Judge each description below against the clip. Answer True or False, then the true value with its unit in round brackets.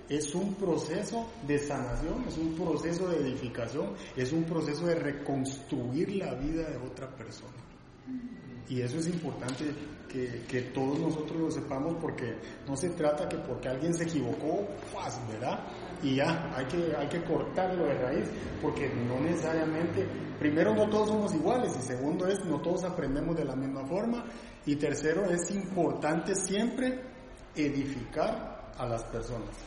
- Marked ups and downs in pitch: False (4.5 semitones)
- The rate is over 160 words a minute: False (155 wpm)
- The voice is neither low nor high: True (150 Hz)